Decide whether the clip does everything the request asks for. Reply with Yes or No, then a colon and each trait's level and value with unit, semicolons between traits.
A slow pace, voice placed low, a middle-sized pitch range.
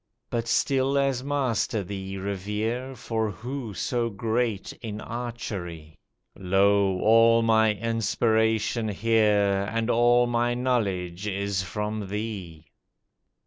Yes: slow, 105 wpm; low, 110 Hz; average, 3.0 semitones